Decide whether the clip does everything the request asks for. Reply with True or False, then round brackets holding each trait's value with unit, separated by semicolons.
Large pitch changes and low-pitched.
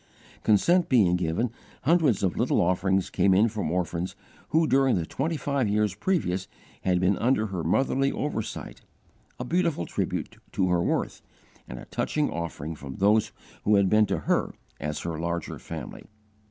True (7.2 semitones; 100 Hz)